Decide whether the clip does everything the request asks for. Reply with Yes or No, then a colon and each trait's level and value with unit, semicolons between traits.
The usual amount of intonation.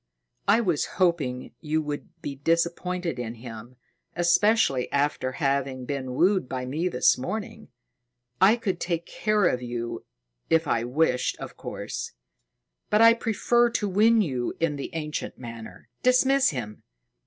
No: wide, 7.3 semitones